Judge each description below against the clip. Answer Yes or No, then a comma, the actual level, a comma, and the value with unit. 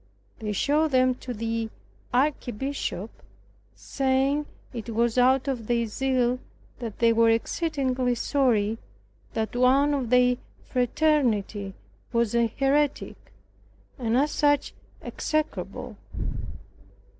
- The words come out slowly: Yes, slow, 110 wpm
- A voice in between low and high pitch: No, very high, 250 Hz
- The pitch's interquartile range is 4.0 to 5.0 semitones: No, average, 3.1 semitones